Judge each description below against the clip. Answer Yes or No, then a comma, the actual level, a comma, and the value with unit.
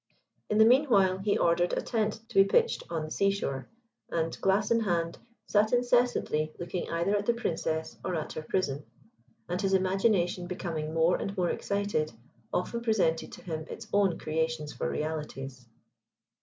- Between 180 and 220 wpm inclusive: No, average, 170 wpm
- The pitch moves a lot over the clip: No, average, 4.3 semitones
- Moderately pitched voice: Yes, medium, 180 Hz